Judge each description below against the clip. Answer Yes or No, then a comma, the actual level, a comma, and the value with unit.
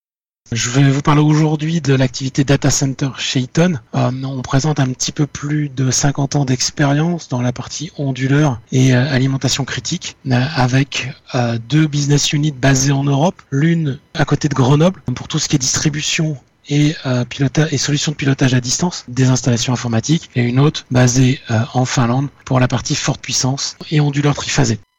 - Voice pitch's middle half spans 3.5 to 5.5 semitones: No, average, 2.7 semitones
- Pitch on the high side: No, medium, 140 Hz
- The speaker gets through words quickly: No, average, 185 wpm